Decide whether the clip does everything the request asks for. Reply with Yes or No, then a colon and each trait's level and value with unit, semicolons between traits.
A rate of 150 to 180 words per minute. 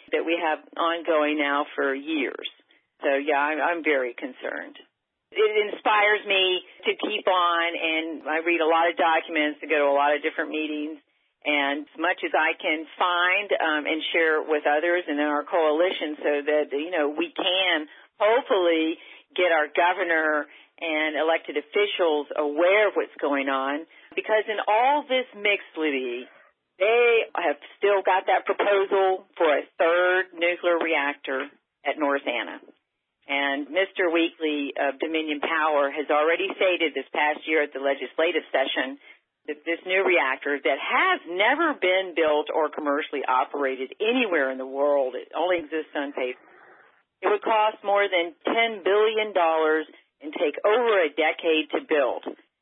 Yes: average, 160 wpm